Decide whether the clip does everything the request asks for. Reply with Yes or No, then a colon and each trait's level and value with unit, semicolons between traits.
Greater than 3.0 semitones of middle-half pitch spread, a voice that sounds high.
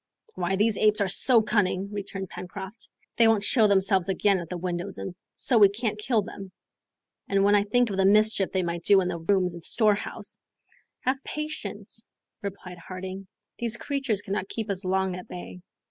No: narrow, 2.4 semitones; high, 200 Hz